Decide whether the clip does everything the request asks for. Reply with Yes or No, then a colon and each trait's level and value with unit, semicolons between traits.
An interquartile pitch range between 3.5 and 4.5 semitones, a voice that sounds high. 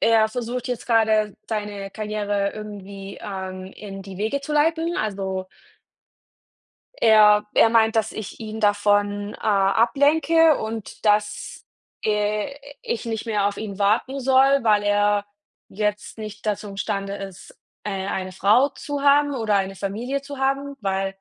No: average, 2.8 semitones; high, 210 Hz